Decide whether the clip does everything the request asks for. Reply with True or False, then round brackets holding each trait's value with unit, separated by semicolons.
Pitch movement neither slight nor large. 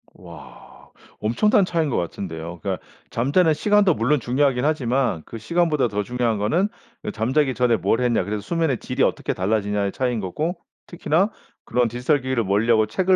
False (6.0 semitones)